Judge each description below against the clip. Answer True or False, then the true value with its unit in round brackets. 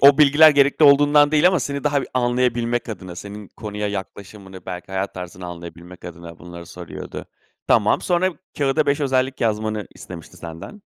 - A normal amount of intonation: False (7.7 semitones)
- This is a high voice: False (110 Hz)